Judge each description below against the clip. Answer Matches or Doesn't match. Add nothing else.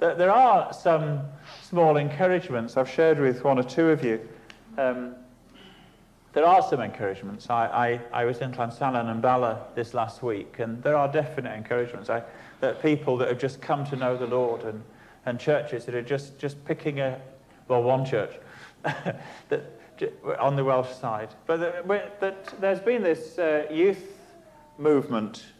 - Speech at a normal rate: Matches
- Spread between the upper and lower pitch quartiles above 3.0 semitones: Matches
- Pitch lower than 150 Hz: Matches